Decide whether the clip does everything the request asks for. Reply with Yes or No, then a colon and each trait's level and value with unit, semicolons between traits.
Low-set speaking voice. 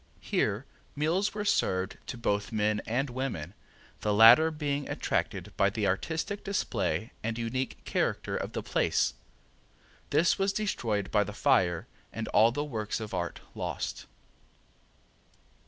Yes: low, 115 Hz